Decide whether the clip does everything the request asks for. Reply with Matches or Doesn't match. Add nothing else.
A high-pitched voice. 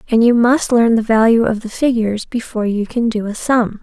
Matches